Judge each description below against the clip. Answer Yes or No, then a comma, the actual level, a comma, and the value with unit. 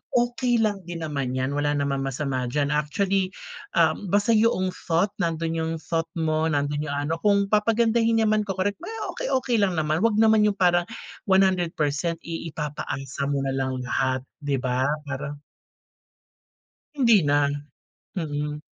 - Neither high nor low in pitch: Yes, medium, 165 Hz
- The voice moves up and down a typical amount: No, wide, 5.9 semitones